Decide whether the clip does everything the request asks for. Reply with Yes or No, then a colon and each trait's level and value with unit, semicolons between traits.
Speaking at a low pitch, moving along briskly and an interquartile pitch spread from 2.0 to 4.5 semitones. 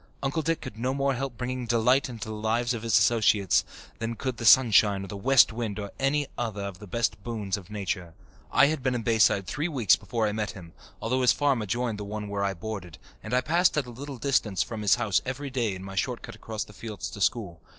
Yes: low, 115 Hz; fast, 245 wpm; average, 3.9 semitones